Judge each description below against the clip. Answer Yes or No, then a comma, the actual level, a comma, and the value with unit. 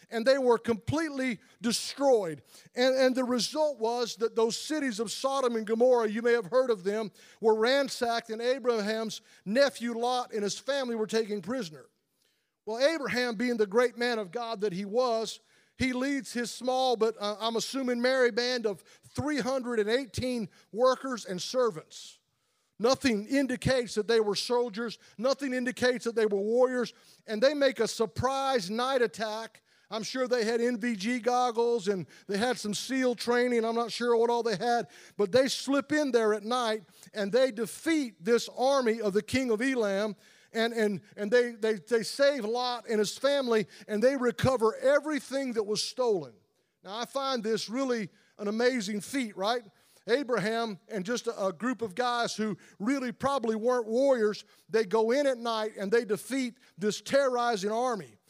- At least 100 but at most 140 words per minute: No, average, 170 wpm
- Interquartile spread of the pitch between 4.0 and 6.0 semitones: No, average, 2.7 semitones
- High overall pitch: Yes, high, 235 Hz